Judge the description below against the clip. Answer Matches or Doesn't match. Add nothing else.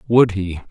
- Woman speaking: Doesn't match